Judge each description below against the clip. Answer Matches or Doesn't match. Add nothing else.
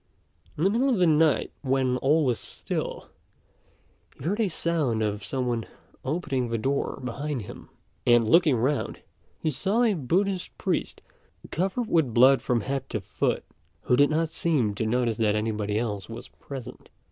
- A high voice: Doesn't match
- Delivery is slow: Doesn't match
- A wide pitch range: Matches